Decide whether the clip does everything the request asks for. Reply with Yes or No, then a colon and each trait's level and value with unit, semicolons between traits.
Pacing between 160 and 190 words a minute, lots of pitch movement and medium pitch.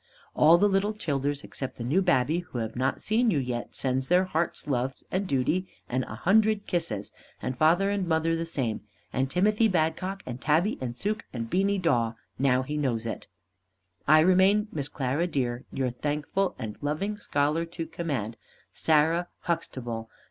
Yes: average, 170 wpm; wide, 6.1 semitones; medium, 155 Hz